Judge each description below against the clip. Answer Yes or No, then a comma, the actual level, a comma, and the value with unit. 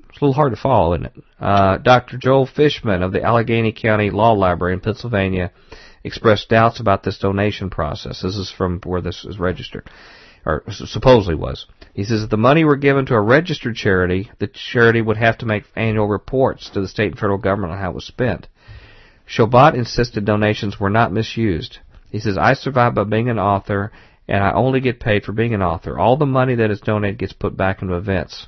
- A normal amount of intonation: Yes, average, 3.5 semitones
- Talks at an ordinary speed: No, fast, 210 wpm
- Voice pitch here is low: Yes, low, 105 Hz